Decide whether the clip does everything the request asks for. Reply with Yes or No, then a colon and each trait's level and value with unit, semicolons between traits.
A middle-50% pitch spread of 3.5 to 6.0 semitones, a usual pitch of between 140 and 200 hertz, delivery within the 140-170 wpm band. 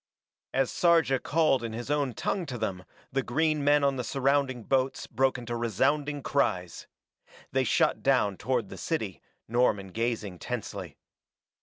No: average, 4.3 semitones; low, 125 Hz; average, 150 wpm